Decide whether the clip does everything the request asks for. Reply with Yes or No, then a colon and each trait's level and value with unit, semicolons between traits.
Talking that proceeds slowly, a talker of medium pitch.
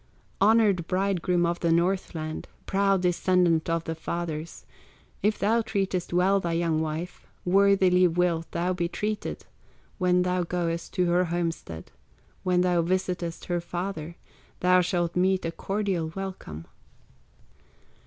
Yes: slow, 130 wpm; medium, 180 Hz